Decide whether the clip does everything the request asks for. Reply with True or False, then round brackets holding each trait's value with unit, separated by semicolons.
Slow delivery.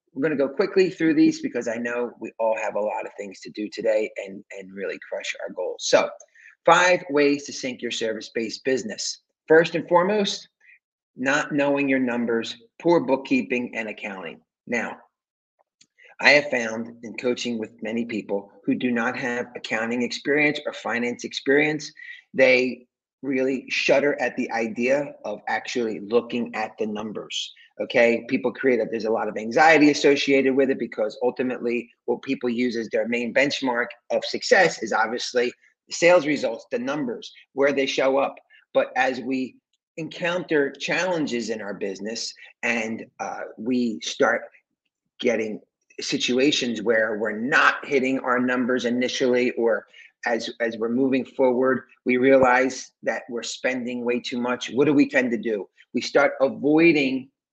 False (160 wpm)